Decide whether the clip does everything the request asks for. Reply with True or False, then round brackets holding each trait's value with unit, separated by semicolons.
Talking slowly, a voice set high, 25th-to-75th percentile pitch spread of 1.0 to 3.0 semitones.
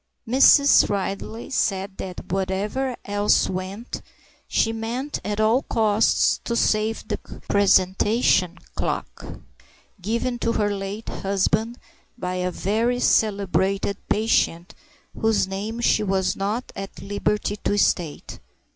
True (115 wpm; 205 Hz; 2.7 semitones)